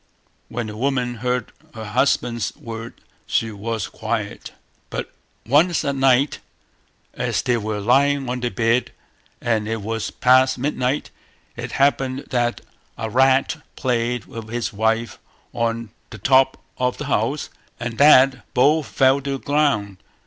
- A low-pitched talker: Yes, low, 125 Hz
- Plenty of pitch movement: No, average, 3.0 semitones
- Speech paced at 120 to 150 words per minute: Yes, average, 140 wpm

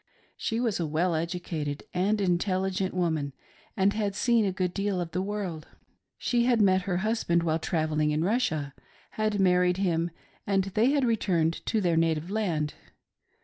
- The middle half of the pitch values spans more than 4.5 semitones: No, average, 3.8 semitones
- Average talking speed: Yes, average, 170 wpm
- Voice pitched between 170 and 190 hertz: Yes, medium, 185 Hz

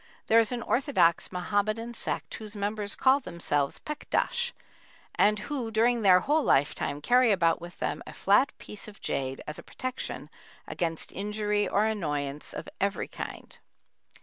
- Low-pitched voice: No, high, 210 Hz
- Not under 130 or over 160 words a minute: Yes, average, 150 wpm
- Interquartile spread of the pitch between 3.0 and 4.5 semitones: No, wide, 5.4 semitones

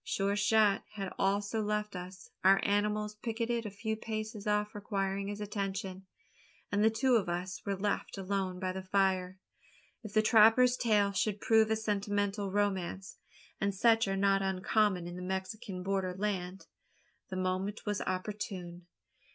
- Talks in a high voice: Yes, high, 200 Hz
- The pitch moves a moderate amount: No, narrow, 1.9 semitones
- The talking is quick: No, average, 155 wpm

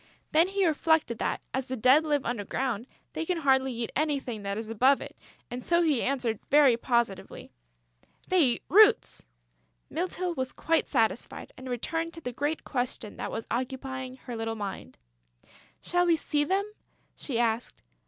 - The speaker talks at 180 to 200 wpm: No, average, 165 wpm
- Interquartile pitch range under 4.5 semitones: No, average, 5.1 semitones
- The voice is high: Yes, very high, 265 Hz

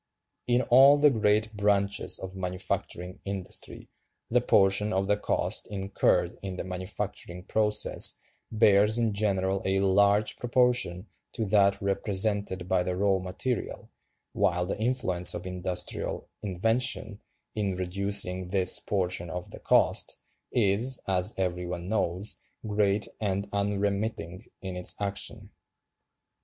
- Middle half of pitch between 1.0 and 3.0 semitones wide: Yes, narrow, 2.4 semitones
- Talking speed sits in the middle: No, slow, 125 wpm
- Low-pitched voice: Yes, low, 100 Hz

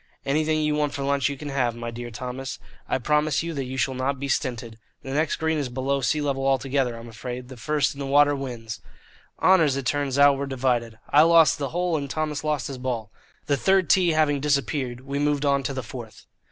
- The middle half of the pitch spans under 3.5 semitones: Yes, average, 2.7 semitones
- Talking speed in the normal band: No, fast, 225 wpm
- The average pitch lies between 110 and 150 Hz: Yes, medium, 140 Hz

